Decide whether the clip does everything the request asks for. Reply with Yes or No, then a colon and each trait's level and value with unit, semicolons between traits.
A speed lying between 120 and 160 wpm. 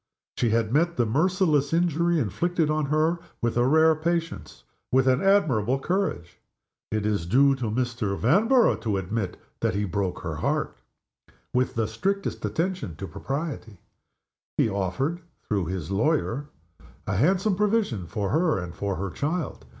Yes: average, 155 wpm